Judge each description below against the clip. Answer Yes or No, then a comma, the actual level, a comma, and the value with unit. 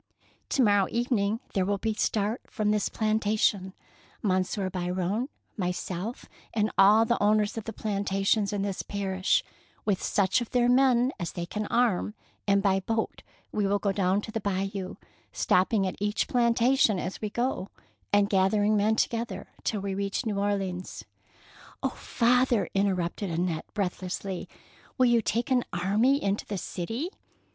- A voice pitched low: No, high, 205 Hz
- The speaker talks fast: No, average, 150 wpm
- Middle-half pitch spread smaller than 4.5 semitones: Yes, average, 2.8 semitones